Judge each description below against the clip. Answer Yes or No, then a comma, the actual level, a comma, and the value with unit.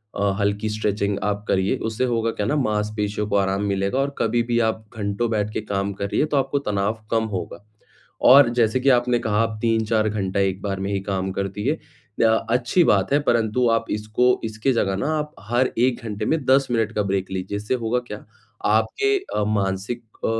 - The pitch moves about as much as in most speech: Yes, average, 3.2 semitones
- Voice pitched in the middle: No, low, 110 Hz